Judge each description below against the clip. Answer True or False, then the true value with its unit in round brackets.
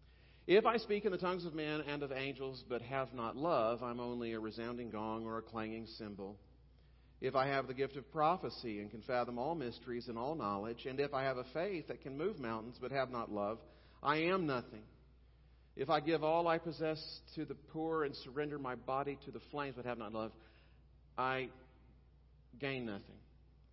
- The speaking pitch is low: True (120 Hz)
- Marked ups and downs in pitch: False (4.4 semitones)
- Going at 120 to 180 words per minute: False (200 wpm)